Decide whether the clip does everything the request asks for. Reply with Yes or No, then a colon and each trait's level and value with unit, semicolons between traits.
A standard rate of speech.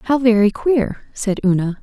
Yes: average, 165 wpm